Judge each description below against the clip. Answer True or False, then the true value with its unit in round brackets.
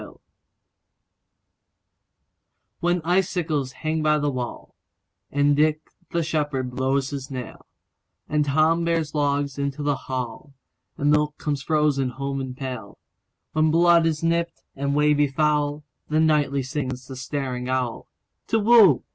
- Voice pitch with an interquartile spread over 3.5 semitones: False (2.6 semitones)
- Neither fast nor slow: False (120 wpm)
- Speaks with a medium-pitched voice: True (145 Hz)